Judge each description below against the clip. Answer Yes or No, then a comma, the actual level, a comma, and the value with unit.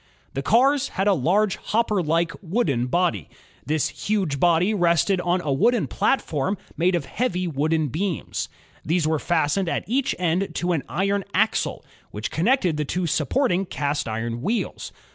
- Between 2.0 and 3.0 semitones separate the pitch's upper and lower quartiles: No, average, 4.7 semitones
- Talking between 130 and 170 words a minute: Yes, average, 160 wpm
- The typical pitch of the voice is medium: Yes, medium, 175 Hz